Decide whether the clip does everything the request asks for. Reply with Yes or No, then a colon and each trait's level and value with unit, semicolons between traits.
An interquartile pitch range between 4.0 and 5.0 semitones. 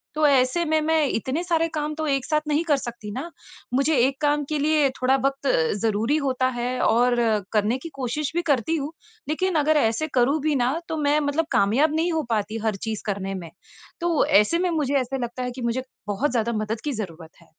Yes: average, 4.5 semitones